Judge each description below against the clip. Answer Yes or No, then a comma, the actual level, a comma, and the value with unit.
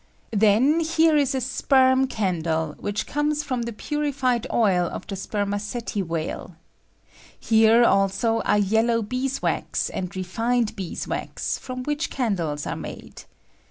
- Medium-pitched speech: No, high, 225 Hz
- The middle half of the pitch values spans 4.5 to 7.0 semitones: Yes, average, 4.9 semitones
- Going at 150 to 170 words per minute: Yes, average, 160 wpm